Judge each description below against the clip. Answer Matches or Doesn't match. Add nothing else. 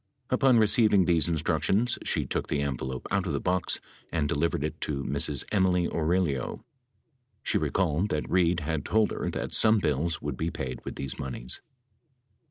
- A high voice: Doesn't match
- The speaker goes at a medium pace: Matches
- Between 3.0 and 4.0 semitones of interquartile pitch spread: Doesn't match